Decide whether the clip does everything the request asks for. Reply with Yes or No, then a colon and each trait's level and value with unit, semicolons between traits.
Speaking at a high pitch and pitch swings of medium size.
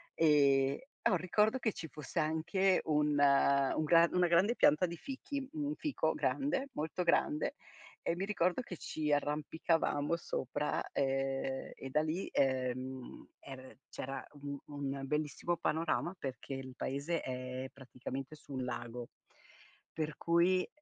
No: medium, 150 Hz; average, 4.3 semitones